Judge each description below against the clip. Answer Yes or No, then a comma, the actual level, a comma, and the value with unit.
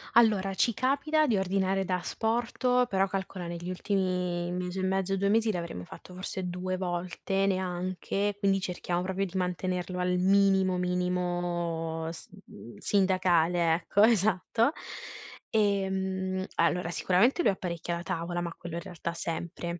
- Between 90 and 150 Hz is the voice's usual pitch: No, medium, 185 Hz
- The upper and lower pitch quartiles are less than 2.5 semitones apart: Yes, narrow, 1.9 semitones